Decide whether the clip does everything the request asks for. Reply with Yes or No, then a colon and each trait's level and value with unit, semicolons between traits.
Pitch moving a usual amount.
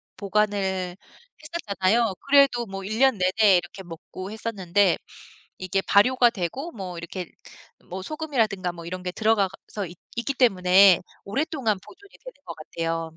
Yes: average, 4.4 semitones